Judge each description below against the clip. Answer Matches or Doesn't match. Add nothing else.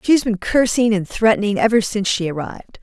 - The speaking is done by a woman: Matches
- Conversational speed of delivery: Doesn't match